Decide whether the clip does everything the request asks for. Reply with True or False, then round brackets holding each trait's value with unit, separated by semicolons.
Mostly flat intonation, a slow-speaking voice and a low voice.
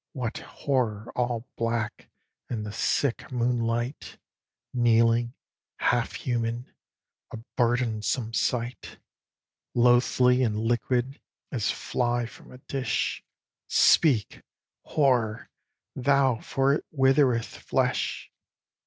True (1.9 semitones; 90 wpm; 120 Hz)